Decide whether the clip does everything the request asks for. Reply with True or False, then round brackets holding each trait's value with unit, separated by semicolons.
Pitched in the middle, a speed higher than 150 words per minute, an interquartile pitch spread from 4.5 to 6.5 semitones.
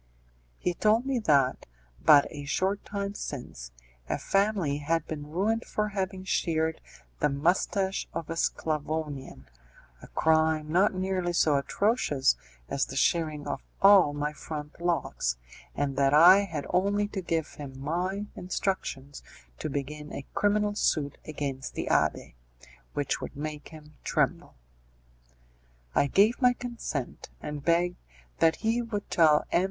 False (160 Hz; 140 wpm; 5.1 semitones)